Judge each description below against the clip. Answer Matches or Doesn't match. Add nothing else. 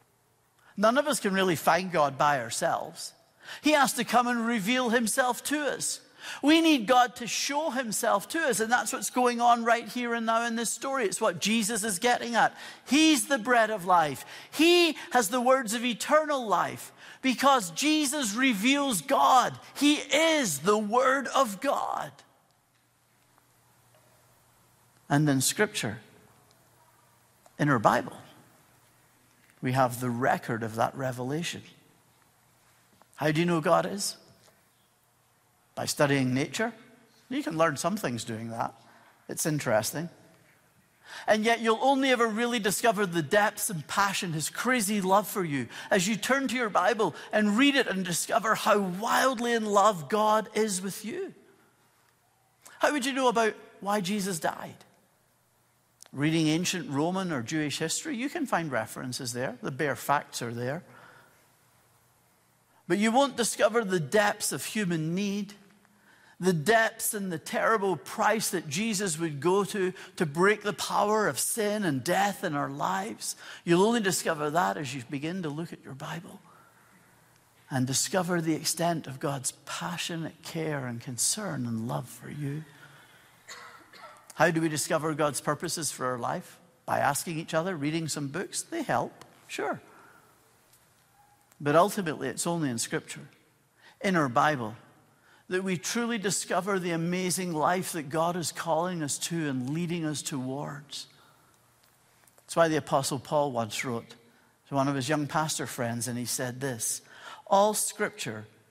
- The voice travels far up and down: Matches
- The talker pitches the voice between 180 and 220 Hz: Matches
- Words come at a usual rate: Matches